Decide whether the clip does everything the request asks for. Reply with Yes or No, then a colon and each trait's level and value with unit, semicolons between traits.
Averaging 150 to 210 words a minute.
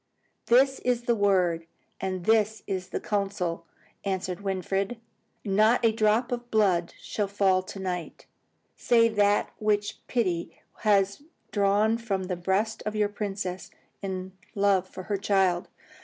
No: average, 140 wpm